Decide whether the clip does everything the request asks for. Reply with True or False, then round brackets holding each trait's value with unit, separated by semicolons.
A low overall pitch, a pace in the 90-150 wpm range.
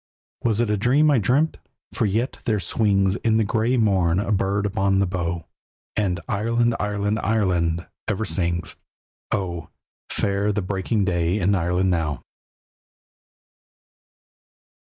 True (100 Hz; 135 wpm)